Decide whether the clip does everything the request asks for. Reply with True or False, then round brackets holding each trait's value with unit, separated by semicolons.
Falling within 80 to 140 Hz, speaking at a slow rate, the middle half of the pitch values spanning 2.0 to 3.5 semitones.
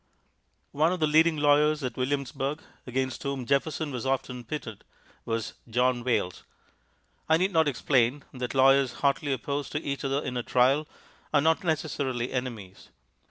False (135 Hz; 155 wpm; 3.0 semitones)